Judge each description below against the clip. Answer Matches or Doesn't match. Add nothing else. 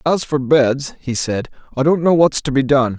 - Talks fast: Matches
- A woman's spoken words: Doesn't match